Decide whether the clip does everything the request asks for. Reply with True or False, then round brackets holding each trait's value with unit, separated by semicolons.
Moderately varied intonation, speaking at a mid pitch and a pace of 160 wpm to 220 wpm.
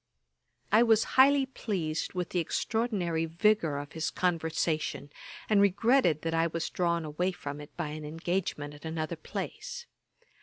False (4.9 semitones; 170 Hz; 150 wpm)